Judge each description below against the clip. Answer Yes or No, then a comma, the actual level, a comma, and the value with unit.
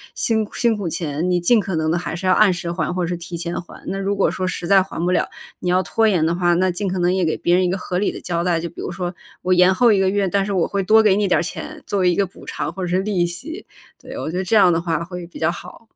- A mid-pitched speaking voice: Yes, medium, 180 Hz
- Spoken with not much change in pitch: Yes, narrow, 2.3 semitones